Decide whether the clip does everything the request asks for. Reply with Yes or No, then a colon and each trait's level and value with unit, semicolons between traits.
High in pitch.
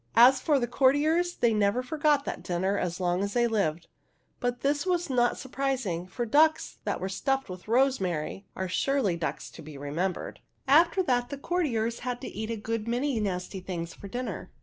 Yes: high, 235 Hz